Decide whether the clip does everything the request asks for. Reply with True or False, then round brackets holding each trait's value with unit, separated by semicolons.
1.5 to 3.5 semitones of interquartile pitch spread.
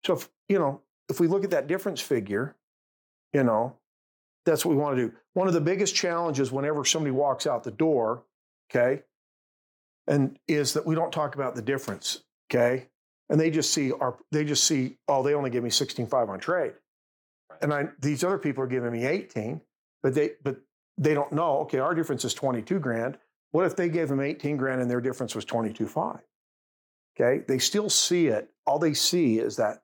False (4.2 semitones)